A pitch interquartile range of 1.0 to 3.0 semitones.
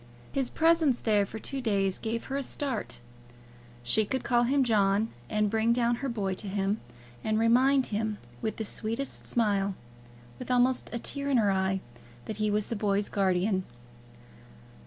No: average, 3.6 semitones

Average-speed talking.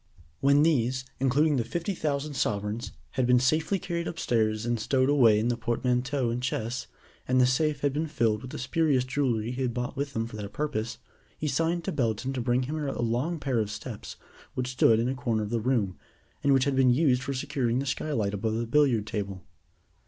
No: fast, 210 wpm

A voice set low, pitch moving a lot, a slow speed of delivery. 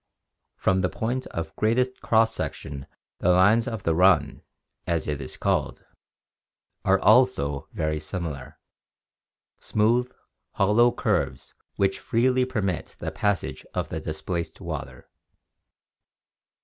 Yes: very low, 95 Hz; wide, 5.8 semitones; slow, 120 wpm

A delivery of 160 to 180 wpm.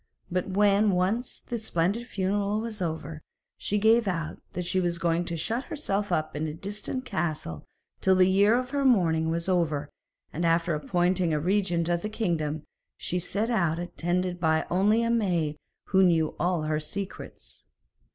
Yes: average, 170 wpm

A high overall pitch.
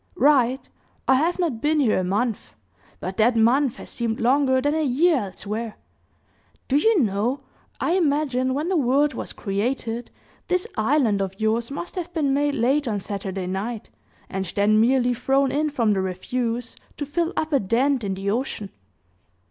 Yes: very high, 250 Hz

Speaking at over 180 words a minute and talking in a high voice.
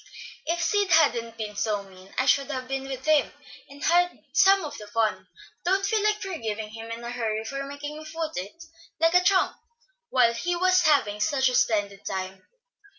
Yes: average, 200 wpm; very high, 270 Hz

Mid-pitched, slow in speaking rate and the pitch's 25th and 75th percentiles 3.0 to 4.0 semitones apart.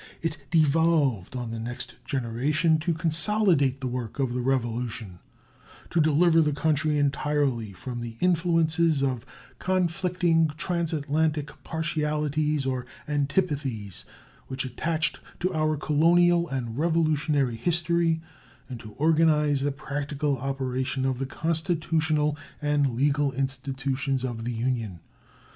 Yes: medium, 145 Hz; slow, 115 wpm; average, 3.7 semitones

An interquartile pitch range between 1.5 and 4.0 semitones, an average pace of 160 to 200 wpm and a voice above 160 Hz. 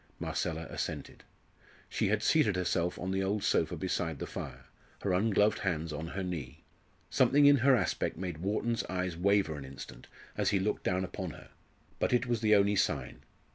No: average, 3.5 semitones; average, 180 wpm; very low, 95 Hz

